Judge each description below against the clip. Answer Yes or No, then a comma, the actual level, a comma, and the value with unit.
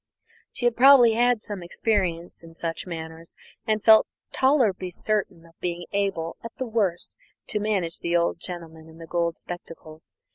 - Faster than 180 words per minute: No, average, 160 wpm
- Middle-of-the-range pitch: Yes, medium, 180 Hz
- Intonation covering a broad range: No, average, 4.6 semitones